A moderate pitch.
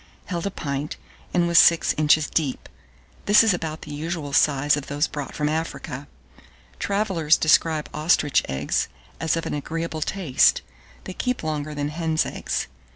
Yes: medium, 155 Hz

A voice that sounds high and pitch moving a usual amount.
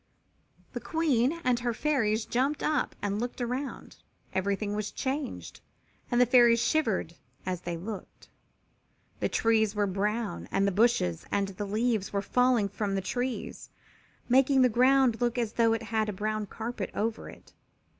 Yes: high, 225 Hz; average, 3.5 semitones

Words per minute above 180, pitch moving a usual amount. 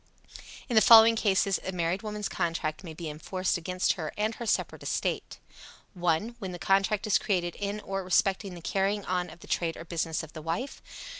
Yes: average, 200 wpm; average, 3.4 semitones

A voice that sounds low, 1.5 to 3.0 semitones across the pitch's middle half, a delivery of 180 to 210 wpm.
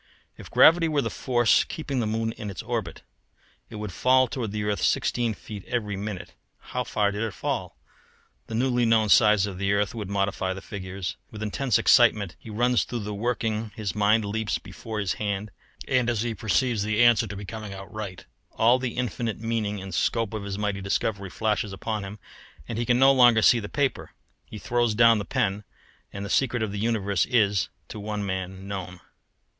Yes: low, 105 Hz; average, 2.7 semitones; average, 200 wpm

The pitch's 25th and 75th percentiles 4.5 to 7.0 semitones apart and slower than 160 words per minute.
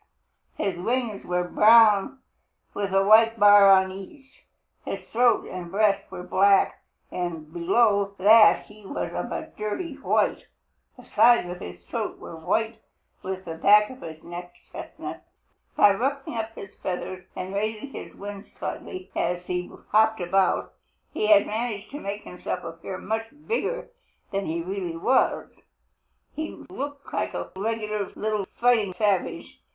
No: average, 3.4 semitones; average, 145 wpm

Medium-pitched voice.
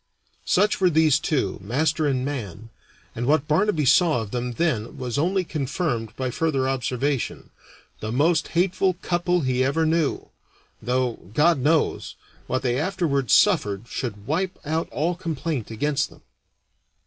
Yes: medium, 145 Hz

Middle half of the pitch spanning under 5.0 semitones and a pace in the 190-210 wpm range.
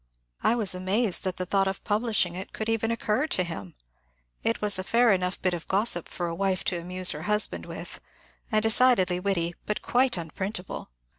Yes: average, 3.4 semitones; average, 195 wpm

